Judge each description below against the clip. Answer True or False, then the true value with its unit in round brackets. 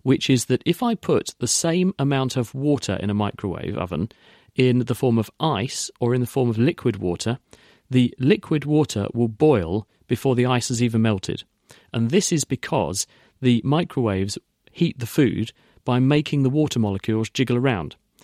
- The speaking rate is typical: True (180 wpm)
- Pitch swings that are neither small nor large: True (3.6 semitones)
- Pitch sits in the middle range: False (125 Hz)